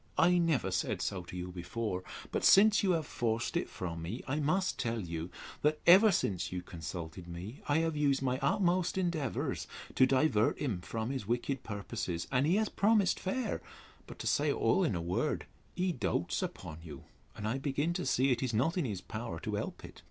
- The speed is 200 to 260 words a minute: Yes, fast, 205 wpm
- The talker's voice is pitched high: No, low, 125 Hz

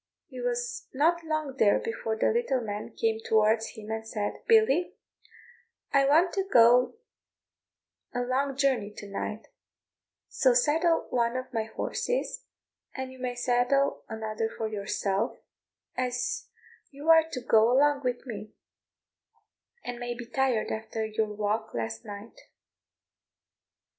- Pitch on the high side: Yes, high, 245 Hz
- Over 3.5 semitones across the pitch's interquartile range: Yes, average, 4.2 semitones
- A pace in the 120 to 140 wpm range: Yes, slow, 135 wpm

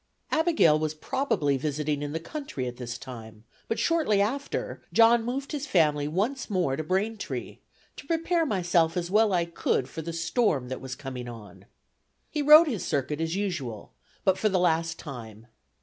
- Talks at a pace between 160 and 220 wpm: Yes, average, 180 wpm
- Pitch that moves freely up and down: Yes, wide, 8.1 semitones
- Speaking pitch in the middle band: Yes, medium, 170 Hz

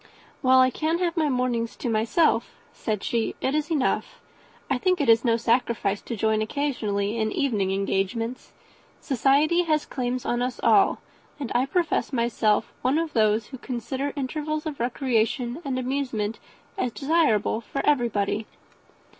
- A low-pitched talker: No, very high, 250 Hz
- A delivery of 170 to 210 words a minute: No, average, 155 wpm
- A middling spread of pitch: Yes, average, 4.2 semitones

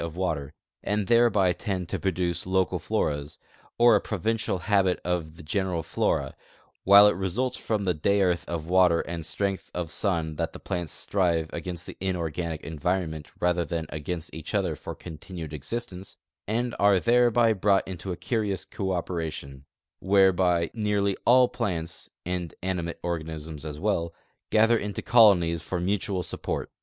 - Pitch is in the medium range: No, very low, 90 Hz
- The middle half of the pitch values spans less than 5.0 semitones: Yes, average, 3.4 semitones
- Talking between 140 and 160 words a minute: Yes, average, 150 wpm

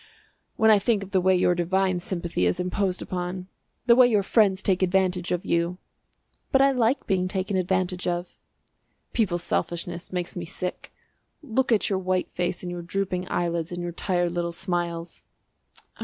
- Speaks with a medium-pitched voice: Yes, medium, 180 Hz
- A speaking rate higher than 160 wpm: Yes, average, 170 wpm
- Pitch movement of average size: No, narrow, 1.8 semitones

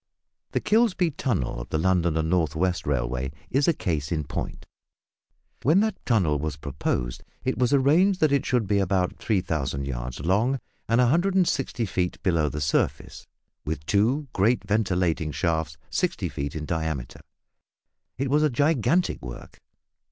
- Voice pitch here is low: Yes, very low, 95 Hz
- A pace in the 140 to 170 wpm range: Yes, average, 150 wpm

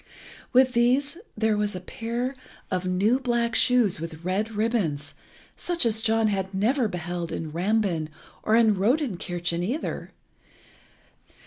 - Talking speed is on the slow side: Yes, slow, 125 wpm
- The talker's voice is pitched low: No, high, 215 Hz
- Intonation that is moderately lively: Yes, average, 4.8 semitones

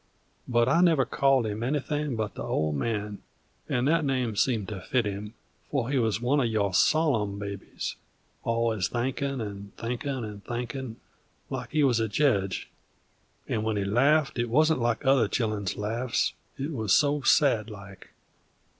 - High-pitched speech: No, low, 120 Hz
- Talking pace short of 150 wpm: No, average, 165 wpm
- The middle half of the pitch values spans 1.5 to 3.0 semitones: No, average, 4.5 semitones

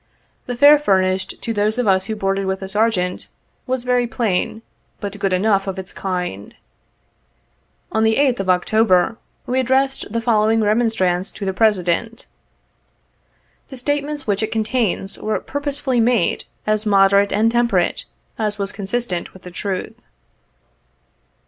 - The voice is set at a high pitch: Yes, high, 215 Hz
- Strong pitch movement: No, average, 3.7 semitones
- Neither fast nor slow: Yes, average, 155 wpm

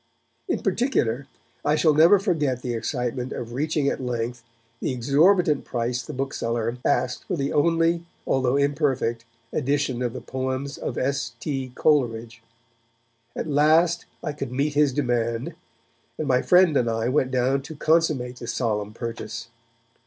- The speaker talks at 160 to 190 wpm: No, average, 150 wpm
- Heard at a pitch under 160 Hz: Yes, low, 135 Hz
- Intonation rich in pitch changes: No, average, 3.7 semitones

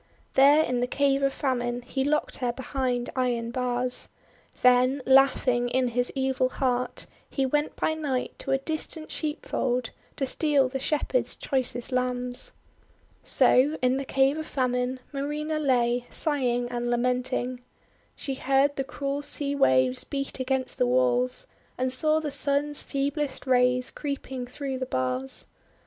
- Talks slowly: No, average, 150 wpm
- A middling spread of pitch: No, narrow, 2.2 semitones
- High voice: Yes, very high, 260 Hz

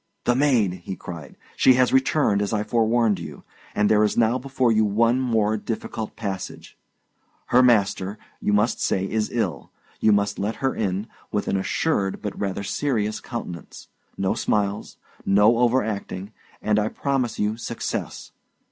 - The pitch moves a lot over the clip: No, average, 2.9 semitones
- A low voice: Yes, low, 110 Hz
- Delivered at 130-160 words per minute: Yes, average, 155 wpm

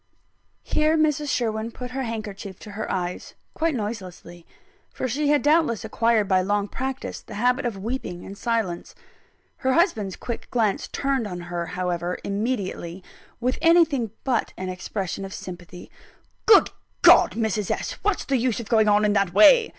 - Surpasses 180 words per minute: No, average, 165 wpm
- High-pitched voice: Yes, high, 220 Hz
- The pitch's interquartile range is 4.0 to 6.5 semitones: Yes, average, 5.2 semitones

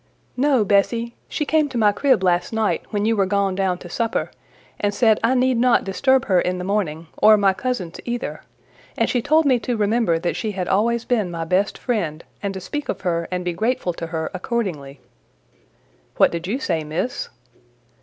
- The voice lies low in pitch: No, high, 205 Hz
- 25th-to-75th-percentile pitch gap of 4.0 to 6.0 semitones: Yes, average, 4.9 semitones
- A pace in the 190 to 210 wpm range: Yes, average, 200 wpm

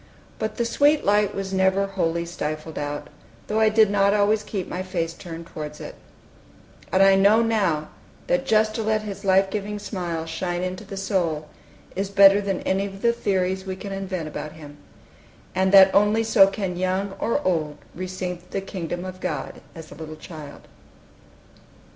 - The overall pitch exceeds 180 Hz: Yes, high, 190 Hz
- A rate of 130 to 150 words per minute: No, average, 175 wpm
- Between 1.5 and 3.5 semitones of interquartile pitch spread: Yes, average, 3.0 semitones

